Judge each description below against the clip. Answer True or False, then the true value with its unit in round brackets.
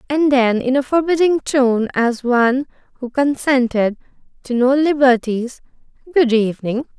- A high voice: True (260 Hz)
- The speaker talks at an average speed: False (130 wpm)